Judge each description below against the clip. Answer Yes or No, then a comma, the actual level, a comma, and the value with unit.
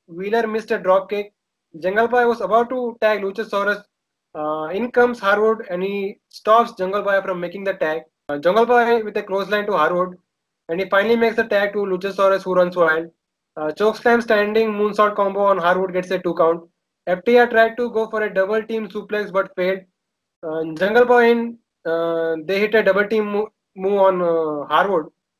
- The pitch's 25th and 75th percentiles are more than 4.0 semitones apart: No, average, 3.3 semitones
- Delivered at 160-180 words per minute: No, average, 190 wpm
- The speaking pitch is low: No, high, 200 Hz